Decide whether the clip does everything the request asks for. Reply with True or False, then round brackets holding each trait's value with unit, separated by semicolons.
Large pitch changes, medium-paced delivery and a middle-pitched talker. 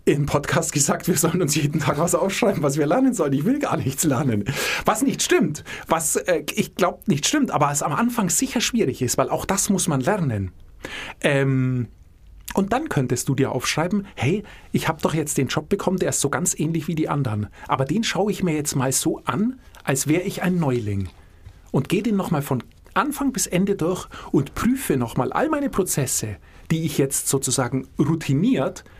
False (5.8 semitones; 205 wpm; 155 Hz)